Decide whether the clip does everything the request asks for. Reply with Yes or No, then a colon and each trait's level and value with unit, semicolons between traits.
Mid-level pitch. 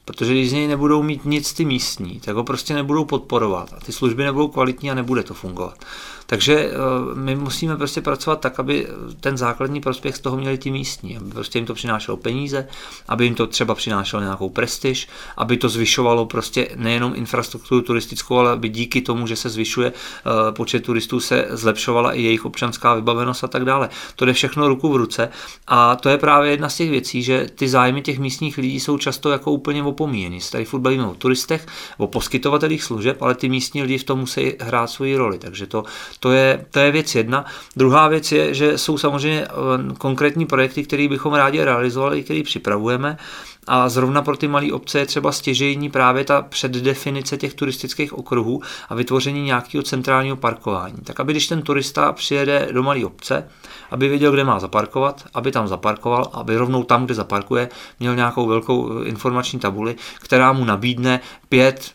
No: low, 130 Hz